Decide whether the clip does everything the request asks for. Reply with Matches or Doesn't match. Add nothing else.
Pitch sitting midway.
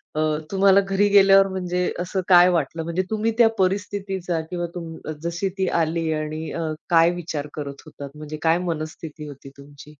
Matches